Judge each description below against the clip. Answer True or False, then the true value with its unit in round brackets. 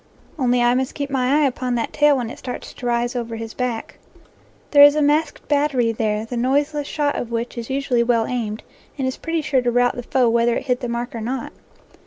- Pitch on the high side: True (250 Hz)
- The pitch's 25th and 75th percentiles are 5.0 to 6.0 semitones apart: False (2.9 semitones)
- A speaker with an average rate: False (235 wpm)